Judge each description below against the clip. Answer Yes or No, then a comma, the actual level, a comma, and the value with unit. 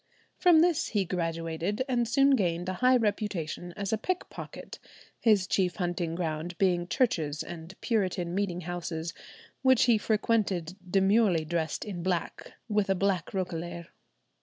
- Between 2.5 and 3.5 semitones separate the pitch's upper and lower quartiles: No, average, 4.0 semitones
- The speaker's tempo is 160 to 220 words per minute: No, average, 140 wpm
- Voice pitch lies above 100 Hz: Yes, medium, 185 Hz